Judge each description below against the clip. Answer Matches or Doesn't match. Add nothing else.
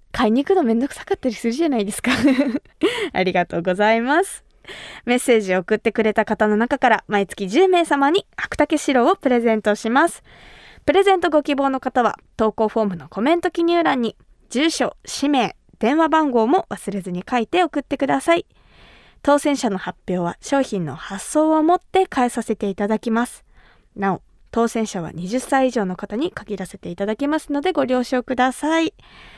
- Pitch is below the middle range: Doesn't match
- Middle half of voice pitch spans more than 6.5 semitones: Doesn't match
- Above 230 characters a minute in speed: Matches